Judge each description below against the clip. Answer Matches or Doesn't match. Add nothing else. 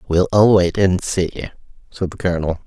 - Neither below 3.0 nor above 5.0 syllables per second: Doesn't match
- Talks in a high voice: Doesn't match